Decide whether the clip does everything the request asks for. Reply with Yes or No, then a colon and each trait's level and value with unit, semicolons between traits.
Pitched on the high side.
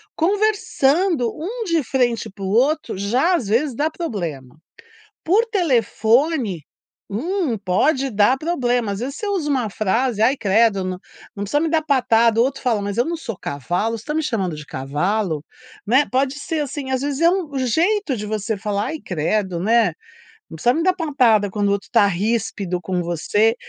Yes: high, 235 Hz